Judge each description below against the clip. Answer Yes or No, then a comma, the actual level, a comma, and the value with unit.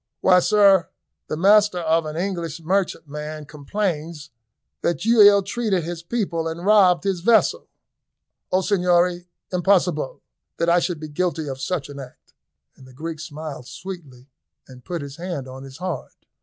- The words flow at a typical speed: Yes, average, 155 wpm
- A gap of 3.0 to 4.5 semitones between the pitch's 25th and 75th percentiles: Yes, average, 3.7 semitones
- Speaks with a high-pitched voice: No, medium, 170 Hz